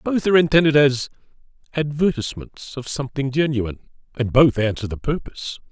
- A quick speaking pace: No, slow, 135 wpm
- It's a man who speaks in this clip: Yes, male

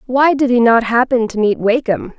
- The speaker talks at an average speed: No, fast, 220 wpm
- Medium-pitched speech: No, high, 240 Hz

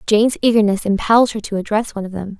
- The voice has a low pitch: No, high, 210 Hz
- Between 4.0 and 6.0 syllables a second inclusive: No, 7.1 syllables/s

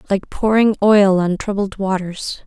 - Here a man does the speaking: No, female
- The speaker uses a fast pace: No, average, 145 wpm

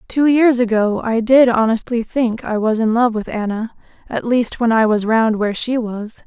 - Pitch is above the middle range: Yes, high, 230 Hz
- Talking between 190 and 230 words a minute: Yes, average, 200 wpm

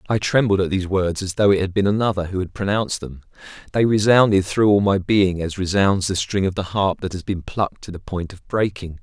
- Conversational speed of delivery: No, fast, 245 wpm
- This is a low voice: Yes, very low, 95 Hz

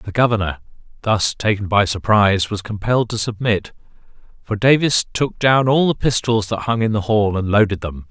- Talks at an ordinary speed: Yes, average, 185 wpm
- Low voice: Yes, low, 105 Hz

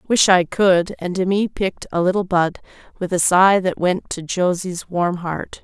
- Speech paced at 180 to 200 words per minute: Yes, average, 190 wpm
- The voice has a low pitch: No, medium, 185 Hz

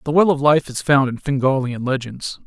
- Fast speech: Yes, fast, 220 wpm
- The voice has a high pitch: No, medium, 140 Hz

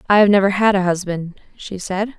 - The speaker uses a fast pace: Yes, fast, 220 wpm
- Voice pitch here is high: Yes, high, 195 Hz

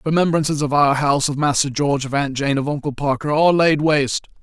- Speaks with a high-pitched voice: No, medium, 145 Hz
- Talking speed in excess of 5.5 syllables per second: Yes, 6.0 syllables/s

